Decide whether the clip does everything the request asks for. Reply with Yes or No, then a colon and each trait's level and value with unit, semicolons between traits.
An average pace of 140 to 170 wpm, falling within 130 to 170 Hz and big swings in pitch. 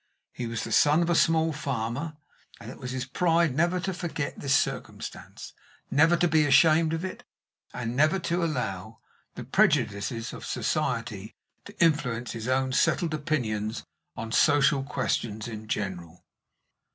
Yes: average, 150 wpm; medium, 140 Hz; wide, 5.9 semitones